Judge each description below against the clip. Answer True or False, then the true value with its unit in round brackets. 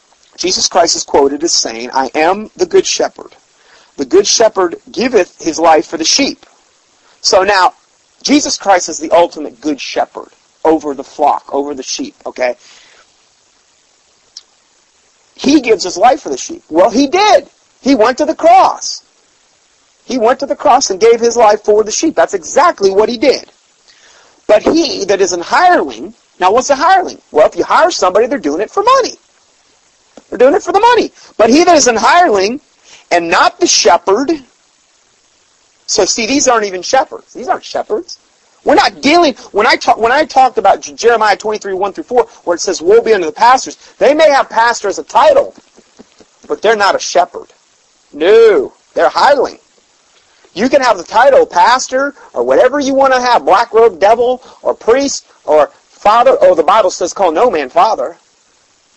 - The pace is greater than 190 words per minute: False (180 wpm)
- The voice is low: False (265 Hz)